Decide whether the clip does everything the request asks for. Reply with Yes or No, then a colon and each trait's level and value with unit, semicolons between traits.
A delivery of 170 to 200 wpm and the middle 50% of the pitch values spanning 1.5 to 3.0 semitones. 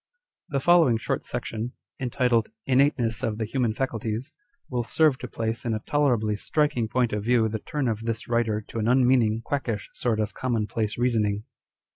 Yes: average, 175 wpm; average, 2.7 semitones